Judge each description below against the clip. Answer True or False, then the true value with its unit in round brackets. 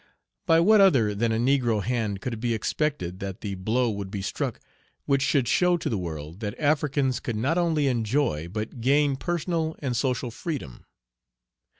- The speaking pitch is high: False (125 Hz)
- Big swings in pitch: True (5.8 semitones)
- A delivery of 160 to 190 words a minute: True (180 wpm)